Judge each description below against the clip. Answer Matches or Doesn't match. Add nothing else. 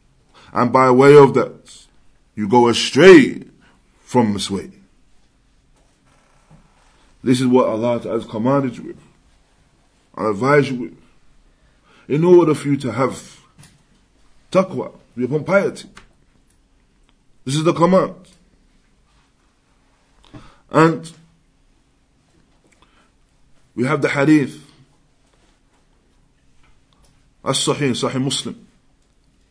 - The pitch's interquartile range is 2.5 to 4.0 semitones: Matches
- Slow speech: Matches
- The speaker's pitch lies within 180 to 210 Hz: Doesn't match